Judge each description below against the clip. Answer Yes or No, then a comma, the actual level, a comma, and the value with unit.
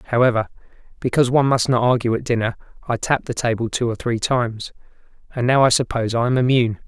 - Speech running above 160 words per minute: Yes, average, 200 wpm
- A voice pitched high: No, low, 120 Hz